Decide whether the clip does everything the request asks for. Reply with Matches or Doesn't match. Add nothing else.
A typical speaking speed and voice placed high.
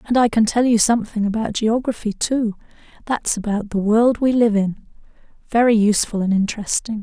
Matches